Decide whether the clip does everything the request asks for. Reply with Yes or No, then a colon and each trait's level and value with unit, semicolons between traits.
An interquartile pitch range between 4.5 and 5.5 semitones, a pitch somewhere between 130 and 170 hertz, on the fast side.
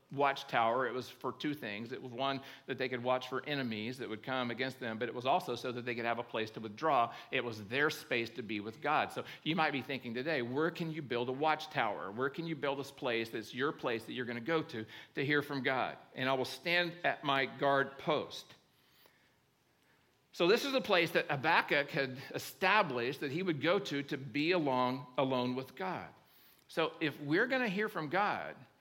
No: average, 3.3 semitones; low, 135 Hz; fast, 225 wpm